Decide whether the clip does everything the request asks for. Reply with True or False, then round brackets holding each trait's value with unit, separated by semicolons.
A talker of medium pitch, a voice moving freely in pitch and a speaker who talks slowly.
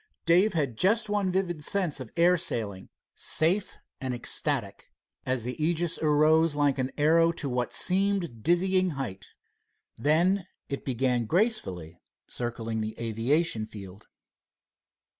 True (150 Hz; 6.8 semitones; 125 wpm)